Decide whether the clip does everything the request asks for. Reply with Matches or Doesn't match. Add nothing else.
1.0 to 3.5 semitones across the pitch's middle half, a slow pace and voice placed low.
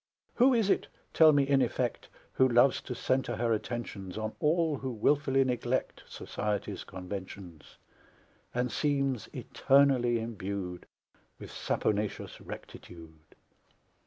Doesn't match